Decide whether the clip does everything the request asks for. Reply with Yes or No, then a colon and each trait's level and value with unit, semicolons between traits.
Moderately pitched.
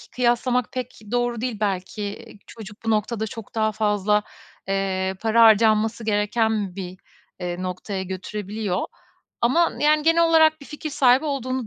No: high, 220 Hz